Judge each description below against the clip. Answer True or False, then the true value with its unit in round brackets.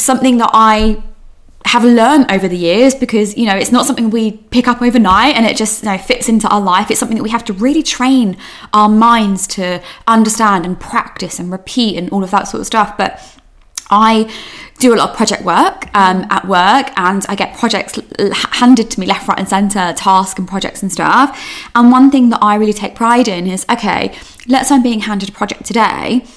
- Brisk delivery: True (220 wpm)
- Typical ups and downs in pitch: True (3.9 semitones)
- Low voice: False (220 Hz)